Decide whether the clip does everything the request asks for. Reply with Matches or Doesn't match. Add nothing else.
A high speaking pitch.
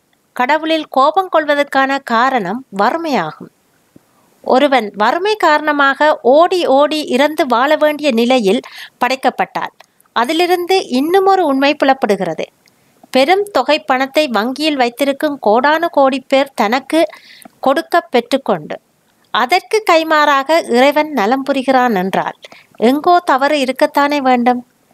Matches